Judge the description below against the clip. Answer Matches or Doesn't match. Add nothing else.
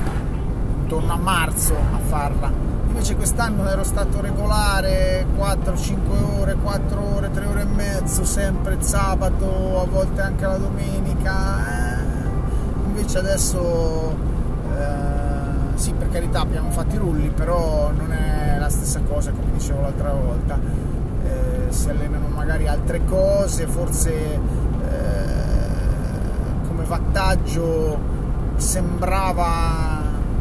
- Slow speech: Matches